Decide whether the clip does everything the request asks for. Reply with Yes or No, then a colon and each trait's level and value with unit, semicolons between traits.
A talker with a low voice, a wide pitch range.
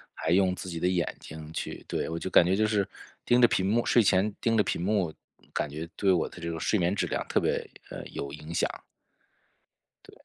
No: very low, 90 Hz; average, 3.9 semitones